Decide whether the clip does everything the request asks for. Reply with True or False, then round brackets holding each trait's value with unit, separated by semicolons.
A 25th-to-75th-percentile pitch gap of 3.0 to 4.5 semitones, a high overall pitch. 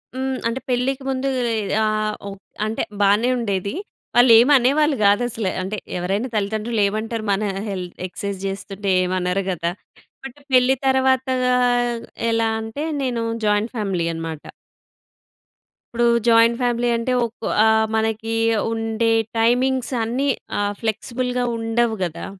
True (3.3 semitones; 225 Hz)